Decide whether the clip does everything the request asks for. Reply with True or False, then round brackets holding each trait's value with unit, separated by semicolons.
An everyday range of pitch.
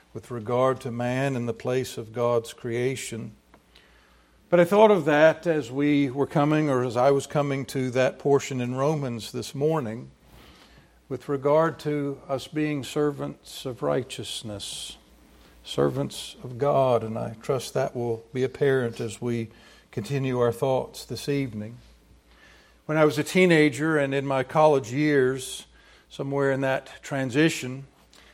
True (3.3 semitones)